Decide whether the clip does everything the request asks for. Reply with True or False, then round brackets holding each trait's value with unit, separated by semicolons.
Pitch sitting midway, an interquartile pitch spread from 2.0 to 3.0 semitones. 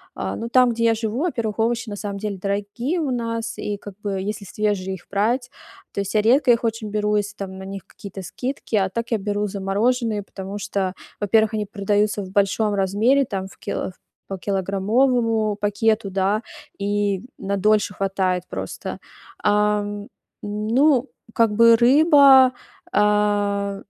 False (210 Hz; 2.5 semitones)